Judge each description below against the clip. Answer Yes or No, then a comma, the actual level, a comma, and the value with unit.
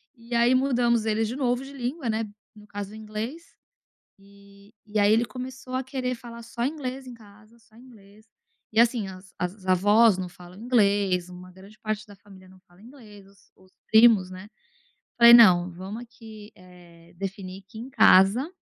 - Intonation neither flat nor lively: Yes, average, 3.6 semitones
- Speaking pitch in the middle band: No, high, 215 Hz